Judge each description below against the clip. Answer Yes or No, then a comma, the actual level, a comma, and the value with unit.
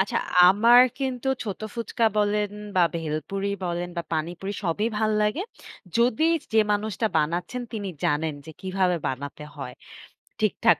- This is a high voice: Yes, high, 195 Hz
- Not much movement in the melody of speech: No, average, 4.6 semitones